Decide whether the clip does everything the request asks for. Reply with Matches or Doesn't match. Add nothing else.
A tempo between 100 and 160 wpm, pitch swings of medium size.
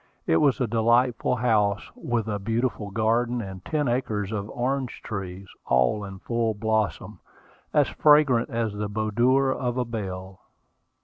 Matches